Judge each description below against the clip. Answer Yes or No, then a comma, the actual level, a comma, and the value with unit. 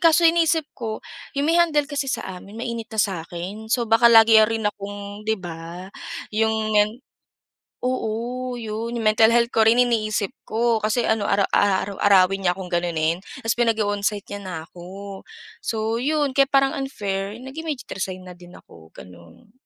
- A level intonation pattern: No, average, 3.7 semitones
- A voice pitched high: Yes, high, 220 Hz